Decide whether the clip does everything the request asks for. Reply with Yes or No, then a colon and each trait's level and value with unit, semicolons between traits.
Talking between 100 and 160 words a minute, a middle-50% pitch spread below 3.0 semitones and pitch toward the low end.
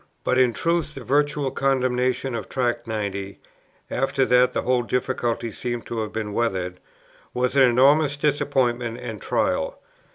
Yes: average, 150 wpm; narrow, 2.5 semitones; low, 125 Hz